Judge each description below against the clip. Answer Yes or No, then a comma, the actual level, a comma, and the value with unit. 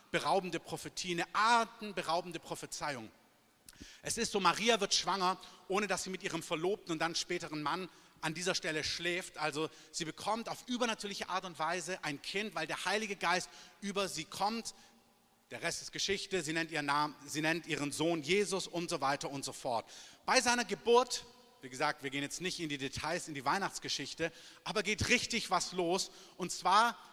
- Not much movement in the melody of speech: No, average, 3.9 semitones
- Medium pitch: Yes, medium, 175 Hz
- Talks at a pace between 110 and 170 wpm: No, average, 185 wpm